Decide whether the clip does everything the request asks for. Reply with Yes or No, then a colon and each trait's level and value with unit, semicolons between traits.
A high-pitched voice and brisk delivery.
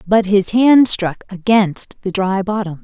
No: high, 200 Hz; average, 170 wpm